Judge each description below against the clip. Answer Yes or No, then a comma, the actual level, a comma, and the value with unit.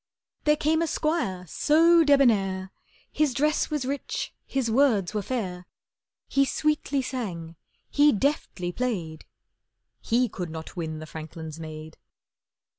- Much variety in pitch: Yes, wide, 8.7 semitones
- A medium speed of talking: No, slow, 125 wpm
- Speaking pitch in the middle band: No, high, 230 Hz